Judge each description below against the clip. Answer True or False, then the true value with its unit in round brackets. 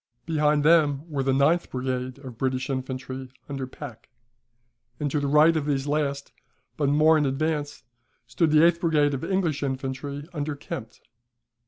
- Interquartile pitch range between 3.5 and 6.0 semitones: False (2.4 semitones)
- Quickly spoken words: False (160 wpm)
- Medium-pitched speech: True (145 Hz)